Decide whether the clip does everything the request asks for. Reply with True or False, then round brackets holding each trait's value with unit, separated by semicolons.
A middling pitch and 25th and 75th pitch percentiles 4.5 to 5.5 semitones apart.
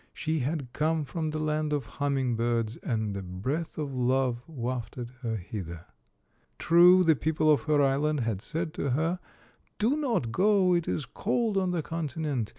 True (150 Hz; 5.2 semitones)